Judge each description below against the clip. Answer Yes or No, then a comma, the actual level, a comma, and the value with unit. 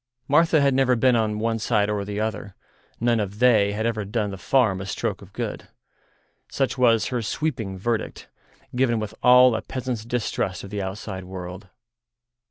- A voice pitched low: Yes, low, 110 Hz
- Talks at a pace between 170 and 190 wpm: Yes, average, 180 wpm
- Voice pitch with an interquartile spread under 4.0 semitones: Yes, average, 3.5 semitones